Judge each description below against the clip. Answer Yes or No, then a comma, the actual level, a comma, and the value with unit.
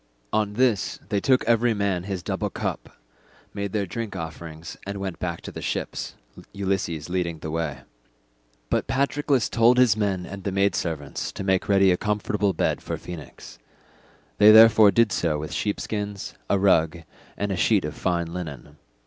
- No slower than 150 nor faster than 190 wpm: Yes, average, 170 wpm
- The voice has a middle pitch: No, low, 100 Hz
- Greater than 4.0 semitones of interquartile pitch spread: No, average, 3.6 semitones